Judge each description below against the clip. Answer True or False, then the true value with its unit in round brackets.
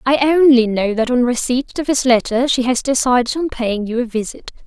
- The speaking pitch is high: True (250 Hz)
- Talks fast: True (220 wpm)